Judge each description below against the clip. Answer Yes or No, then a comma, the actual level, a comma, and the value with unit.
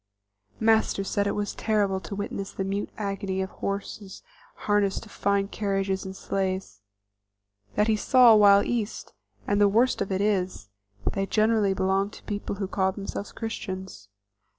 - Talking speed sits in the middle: Yes, average, 155 wpm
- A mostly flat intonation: Yes, narrow, 1.5 semitones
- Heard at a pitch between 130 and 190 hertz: No, high, 200 Hz